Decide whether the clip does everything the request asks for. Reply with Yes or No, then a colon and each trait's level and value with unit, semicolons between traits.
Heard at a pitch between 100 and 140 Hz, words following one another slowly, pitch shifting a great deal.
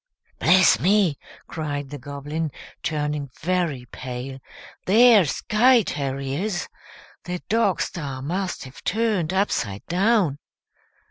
No: medium, 165 Hz; slow, 105 wpm; wide, 5.7 semitones